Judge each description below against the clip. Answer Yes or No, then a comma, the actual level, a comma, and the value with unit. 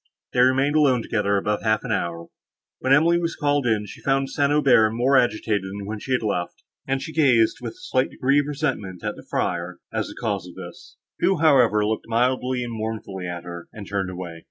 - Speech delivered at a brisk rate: Yes, fast, 220 wpm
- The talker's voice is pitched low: Yes, low, 115 Hz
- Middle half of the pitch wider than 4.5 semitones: Yes, average, 5.1 semitones